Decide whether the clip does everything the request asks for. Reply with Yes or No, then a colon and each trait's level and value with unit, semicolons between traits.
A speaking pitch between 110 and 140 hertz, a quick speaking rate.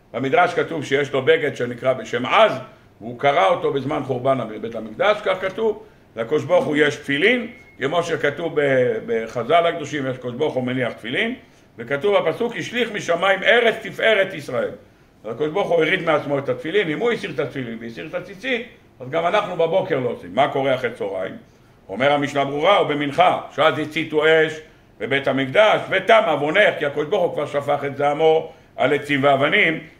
No: medium, 150 Hz; fast, 165 wpm